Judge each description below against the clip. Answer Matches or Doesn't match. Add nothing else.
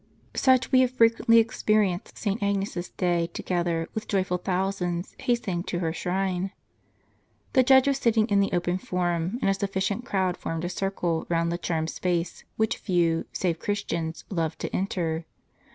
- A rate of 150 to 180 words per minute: Matches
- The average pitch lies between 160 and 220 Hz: Matches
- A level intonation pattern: Doesn't match